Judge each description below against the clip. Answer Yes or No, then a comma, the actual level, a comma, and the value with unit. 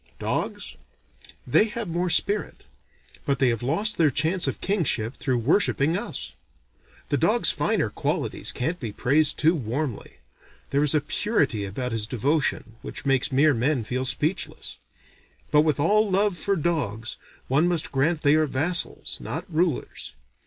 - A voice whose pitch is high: No, medium, 150 Hz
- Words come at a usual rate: Yes, average, 150 wpm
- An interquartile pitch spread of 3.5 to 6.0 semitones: Yes, average, 5.0 semitones